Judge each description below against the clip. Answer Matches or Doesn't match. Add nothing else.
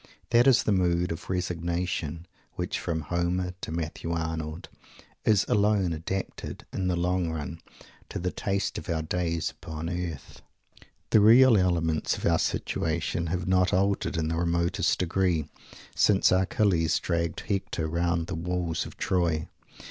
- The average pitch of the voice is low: Matches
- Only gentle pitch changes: Matches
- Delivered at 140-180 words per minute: Matches